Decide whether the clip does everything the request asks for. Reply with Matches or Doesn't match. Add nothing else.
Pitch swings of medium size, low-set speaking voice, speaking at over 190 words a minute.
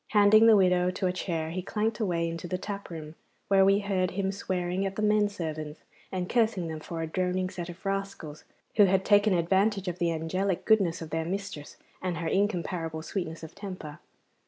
Doesn't match